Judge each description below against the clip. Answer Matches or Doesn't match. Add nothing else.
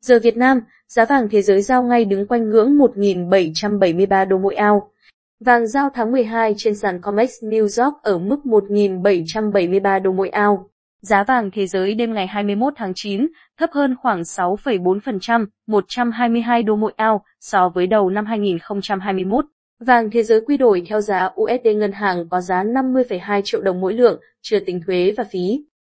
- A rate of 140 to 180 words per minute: Matches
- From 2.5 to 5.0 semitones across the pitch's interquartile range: Matches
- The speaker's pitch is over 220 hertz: Doesn't match